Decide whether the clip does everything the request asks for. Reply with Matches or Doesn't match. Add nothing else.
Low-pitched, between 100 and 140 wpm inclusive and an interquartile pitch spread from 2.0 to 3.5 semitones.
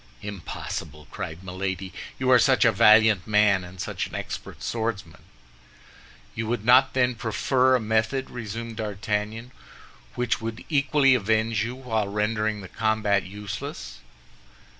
Matches